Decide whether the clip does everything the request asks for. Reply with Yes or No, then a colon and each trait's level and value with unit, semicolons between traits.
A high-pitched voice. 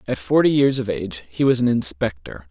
No: low, 105 Hz